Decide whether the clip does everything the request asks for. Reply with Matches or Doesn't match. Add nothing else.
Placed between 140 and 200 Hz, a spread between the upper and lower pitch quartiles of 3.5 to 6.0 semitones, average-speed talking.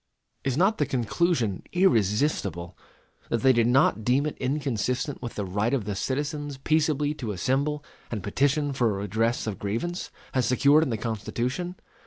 Doesn't match